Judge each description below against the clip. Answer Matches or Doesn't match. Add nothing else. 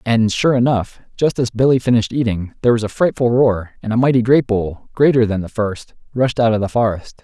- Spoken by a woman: Doesn't match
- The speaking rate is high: Matches